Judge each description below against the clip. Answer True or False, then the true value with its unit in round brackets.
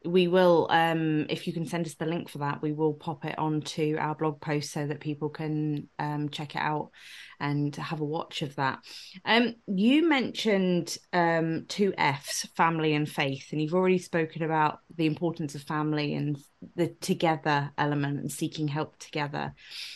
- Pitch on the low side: False (155 Hz)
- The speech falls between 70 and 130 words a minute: False (180 wpm)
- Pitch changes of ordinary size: False (2.3 semitones)